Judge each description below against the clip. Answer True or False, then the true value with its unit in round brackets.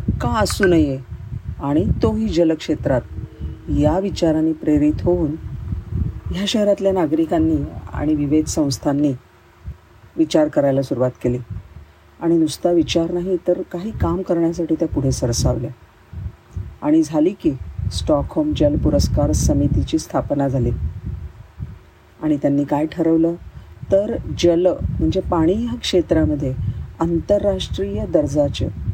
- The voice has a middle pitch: True (145 Hz)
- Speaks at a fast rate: False (110 wpm)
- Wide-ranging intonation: True (8.3 semitones)